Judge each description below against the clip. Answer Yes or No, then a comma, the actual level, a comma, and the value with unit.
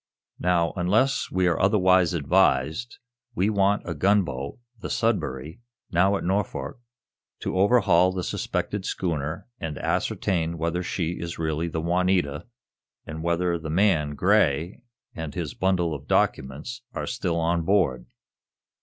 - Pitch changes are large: No, average, 3.1 semitones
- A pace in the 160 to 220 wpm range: No, slow, 135 wpm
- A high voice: No, very low, 85 Hz